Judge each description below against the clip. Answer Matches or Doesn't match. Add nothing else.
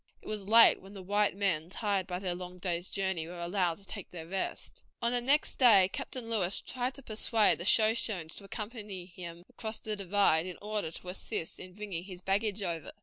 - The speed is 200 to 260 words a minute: Matches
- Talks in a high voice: Matches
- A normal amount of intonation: Matches